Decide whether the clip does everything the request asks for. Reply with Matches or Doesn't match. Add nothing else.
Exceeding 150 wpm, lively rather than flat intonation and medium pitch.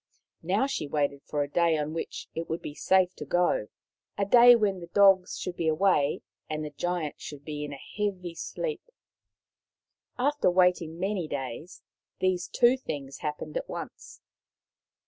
Doesn't match